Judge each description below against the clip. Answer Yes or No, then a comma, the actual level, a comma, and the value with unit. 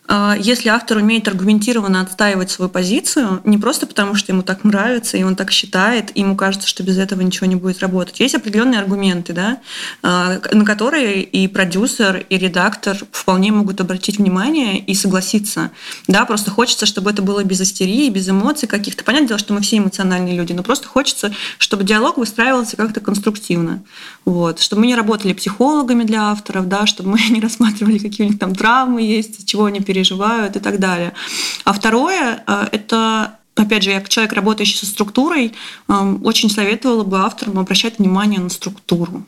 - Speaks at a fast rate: Yes, fast, 175 wpm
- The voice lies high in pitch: Yes, high, 210 Hz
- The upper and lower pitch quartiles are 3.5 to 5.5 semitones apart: No, average, 2.8 semitones